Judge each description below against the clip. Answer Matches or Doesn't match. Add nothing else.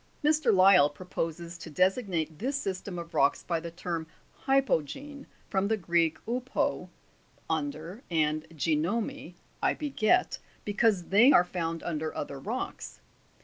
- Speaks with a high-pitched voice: Doesn't match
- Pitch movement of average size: Doesn't match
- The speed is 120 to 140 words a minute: Matches